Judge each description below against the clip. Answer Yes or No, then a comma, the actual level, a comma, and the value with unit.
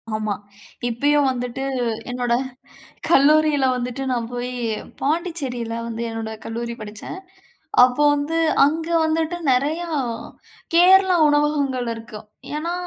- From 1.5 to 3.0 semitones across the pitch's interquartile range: No, average, 4.7 semitones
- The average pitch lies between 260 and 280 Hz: Yes, very high, 270 Hz